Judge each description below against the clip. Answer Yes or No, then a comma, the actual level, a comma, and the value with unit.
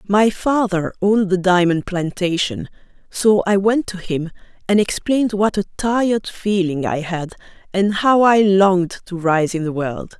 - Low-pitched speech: No, high, 190 Hz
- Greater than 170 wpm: No, average, 165 wpm